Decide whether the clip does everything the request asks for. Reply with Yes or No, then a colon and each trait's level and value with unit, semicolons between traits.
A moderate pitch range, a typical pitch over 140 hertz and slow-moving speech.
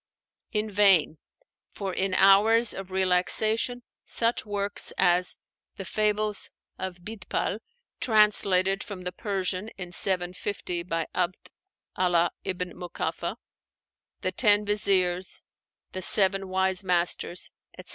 No: narrow, 2.3 semitones; high, 190 Hz; slow, 110 wpm